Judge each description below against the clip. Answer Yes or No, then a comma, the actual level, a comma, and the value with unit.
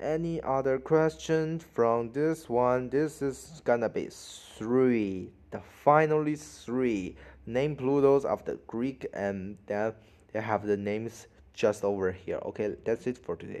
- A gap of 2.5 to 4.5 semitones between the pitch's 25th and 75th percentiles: No, wide, 5.6 semitones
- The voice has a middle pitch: No, low, 125 Hz